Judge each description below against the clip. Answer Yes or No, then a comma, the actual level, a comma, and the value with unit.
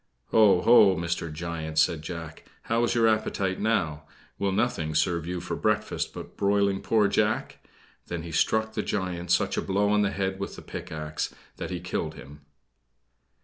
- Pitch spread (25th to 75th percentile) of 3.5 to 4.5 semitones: Yes, average, 4.0 semitones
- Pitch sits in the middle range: No, very low, 95 Hz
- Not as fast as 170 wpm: No, average, 175 wpm